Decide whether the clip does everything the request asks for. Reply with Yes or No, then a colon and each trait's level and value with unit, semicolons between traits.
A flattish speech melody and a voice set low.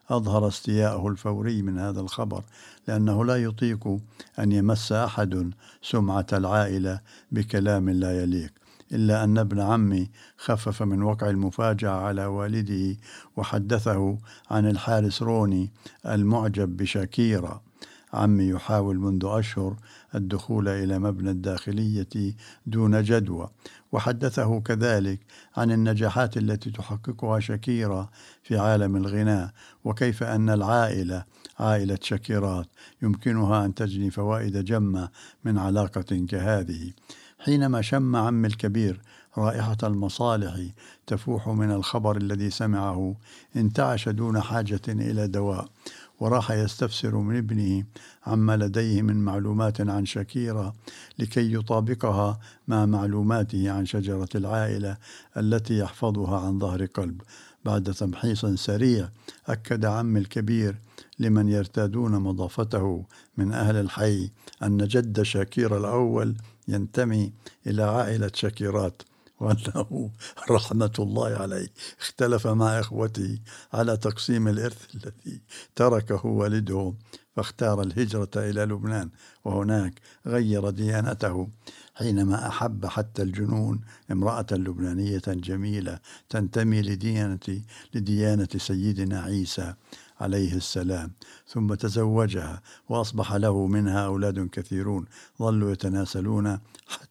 Yes: narrow, 2.1 semitones; low, 105 Hz